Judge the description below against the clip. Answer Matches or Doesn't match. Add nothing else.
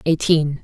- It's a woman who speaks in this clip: Matches